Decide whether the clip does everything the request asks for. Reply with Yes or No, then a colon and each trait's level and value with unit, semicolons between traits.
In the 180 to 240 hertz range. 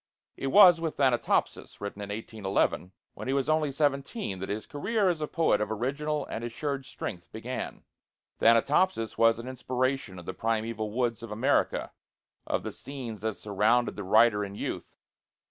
No: low, 120 Hz